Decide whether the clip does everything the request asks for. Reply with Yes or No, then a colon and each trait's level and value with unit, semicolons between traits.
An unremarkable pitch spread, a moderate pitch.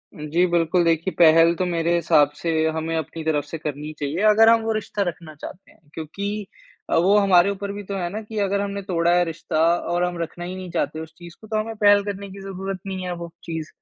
Yes: average, 3.4 semitones; medium, 175 Hz